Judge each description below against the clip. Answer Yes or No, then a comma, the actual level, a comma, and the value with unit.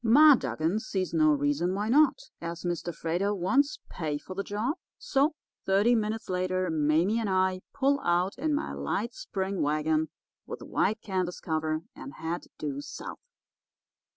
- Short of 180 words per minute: Yes, average, 155 wpm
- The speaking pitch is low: No, medium, 185 Hz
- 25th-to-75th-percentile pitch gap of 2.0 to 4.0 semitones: No, wide, 5.6 semitones